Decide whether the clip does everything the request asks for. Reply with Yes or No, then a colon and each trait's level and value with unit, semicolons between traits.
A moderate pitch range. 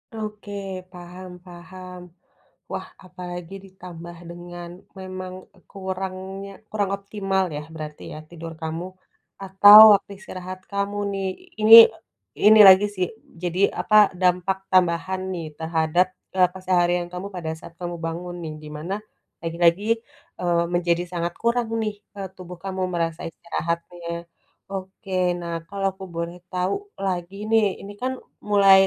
No: narrow, 1.9 semitones